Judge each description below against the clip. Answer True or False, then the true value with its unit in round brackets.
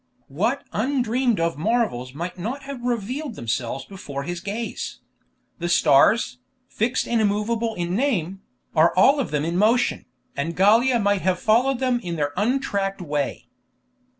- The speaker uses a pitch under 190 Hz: False (205 Hz)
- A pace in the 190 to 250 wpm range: False (150 wpm)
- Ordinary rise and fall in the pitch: False (6.1 semitones)